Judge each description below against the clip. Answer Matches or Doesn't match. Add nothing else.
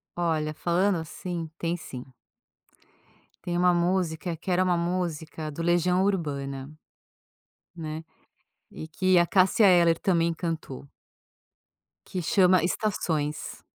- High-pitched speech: Doesn't match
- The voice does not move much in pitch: Matches